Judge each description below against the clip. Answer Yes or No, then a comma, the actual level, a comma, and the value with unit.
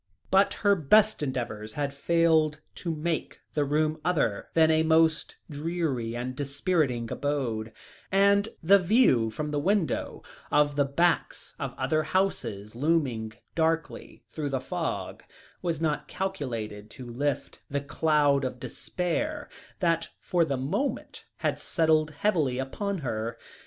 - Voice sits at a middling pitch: Yes, medium, 150 Hz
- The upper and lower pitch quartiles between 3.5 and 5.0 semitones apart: Yes, average, 4.3 semitones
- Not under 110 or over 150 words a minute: Yes, slow, 135 wpm